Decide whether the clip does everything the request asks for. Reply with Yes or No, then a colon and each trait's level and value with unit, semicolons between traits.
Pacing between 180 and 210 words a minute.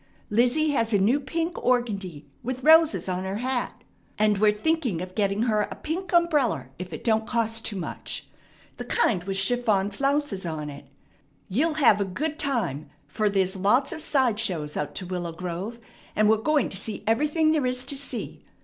Yes: average, 185 wpm